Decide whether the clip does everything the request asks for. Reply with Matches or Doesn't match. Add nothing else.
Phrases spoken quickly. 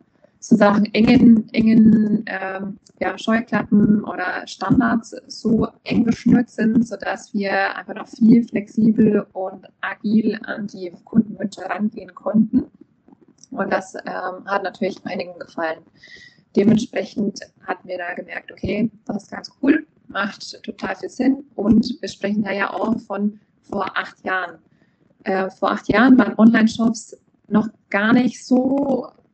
Doesn't match